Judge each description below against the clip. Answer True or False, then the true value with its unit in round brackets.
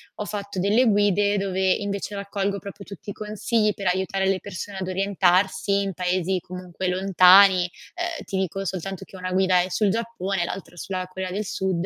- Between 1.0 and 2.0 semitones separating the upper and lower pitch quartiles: True (1.6 semitones)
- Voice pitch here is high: True (195 Hz)